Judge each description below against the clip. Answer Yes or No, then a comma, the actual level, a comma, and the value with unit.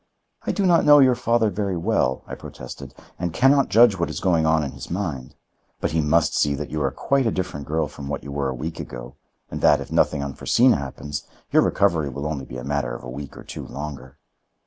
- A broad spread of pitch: Yes, wide, 6.0 semitones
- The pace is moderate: No, fast, 235 wpm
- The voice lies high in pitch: No, very low, 75 Hz